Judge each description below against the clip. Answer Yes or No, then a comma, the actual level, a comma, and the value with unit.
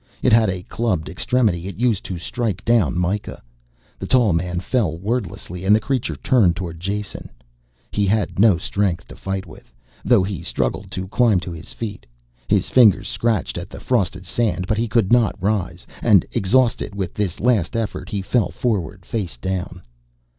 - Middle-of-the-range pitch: No, low, 100 Hz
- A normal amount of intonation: Yes, average, 4.1 semitones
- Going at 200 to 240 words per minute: No, average, 175 wpm